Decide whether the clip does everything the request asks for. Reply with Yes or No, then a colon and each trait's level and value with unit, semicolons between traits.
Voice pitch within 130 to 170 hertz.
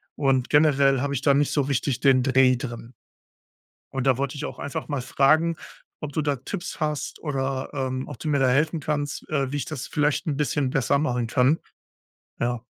Yes: medium, 140 Hz